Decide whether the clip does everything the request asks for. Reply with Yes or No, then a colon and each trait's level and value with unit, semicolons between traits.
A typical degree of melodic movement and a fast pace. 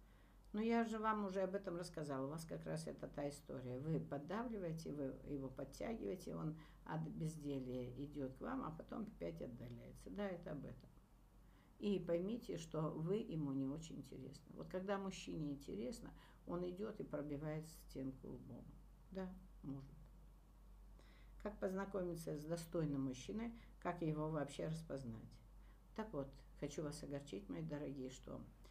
No: average, 5.0 semitones; average, 150 wpm